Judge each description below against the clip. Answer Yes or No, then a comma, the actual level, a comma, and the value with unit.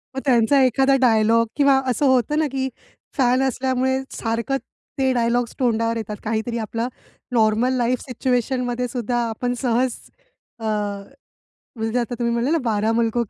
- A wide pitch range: No, narrow, 2.4 semitones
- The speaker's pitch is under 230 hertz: No, high, 245 Hz